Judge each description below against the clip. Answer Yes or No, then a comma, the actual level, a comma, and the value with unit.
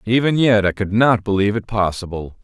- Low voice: Yes, low, 105 Hz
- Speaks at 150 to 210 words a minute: Yes, average, 200 wpm